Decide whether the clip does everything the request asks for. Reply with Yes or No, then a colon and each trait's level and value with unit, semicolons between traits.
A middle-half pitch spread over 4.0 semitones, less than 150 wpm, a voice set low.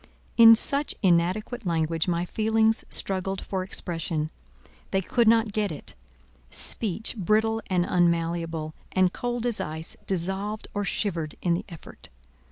No: average, 4.5 semitones; slow, 135 wpm; high, 190 Hz